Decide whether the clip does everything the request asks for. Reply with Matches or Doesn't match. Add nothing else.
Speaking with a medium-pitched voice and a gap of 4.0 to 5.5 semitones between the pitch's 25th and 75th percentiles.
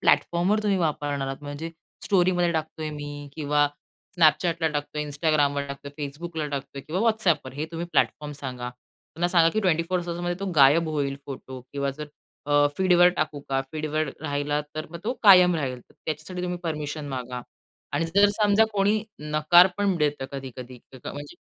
Doesn't match